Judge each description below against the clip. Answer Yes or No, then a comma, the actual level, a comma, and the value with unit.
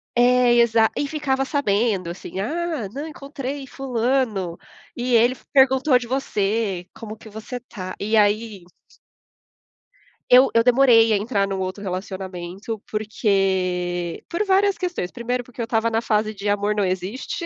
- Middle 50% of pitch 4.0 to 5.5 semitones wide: Yes, average, 4.5 semitones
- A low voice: No, high, 225 Hz